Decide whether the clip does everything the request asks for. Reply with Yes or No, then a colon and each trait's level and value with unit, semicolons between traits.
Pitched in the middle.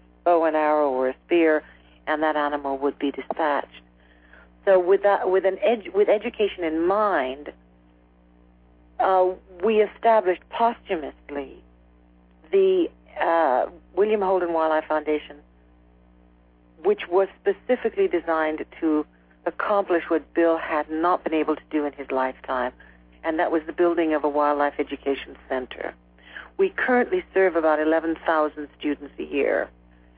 Yes: medium, 155 Hz